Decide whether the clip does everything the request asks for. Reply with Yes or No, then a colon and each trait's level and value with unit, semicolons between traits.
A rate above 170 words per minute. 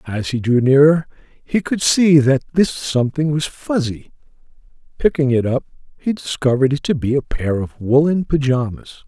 No: average, 165 wpm